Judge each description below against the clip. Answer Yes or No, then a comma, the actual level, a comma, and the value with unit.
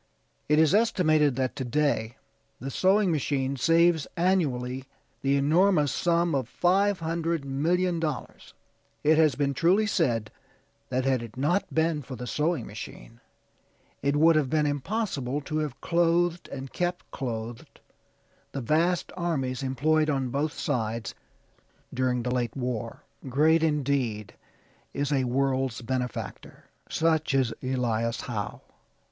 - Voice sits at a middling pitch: Yes, medium, 145 Hz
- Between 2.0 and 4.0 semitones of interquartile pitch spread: No, average, 4.4 semitones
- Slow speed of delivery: Yes, slow, 130 wpm